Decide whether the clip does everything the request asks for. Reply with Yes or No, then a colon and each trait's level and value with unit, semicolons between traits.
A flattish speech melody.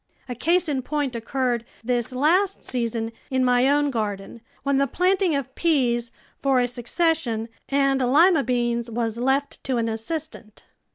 No: average, 3.5 semitones